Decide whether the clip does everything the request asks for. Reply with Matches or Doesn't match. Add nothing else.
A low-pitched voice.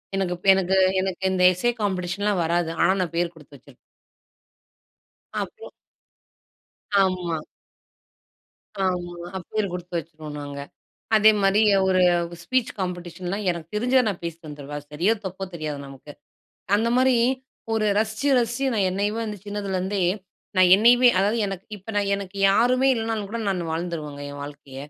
Doesn't match